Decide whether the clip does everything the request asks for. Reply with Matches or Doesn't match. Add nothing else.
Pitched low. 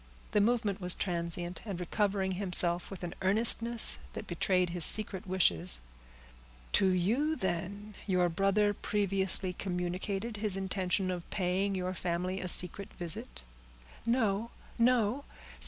Doesn't match